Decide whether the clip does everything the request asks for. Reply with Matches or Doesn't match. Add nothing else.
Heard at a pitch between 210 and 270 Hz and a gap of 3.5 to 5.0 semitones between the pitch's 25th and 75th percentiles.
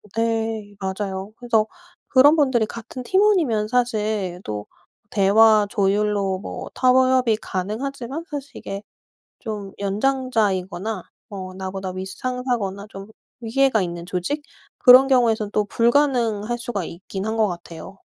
Matches